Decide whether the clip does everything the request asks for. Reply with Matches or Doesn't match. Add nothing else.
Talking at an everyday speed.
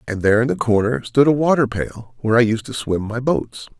Doesn't match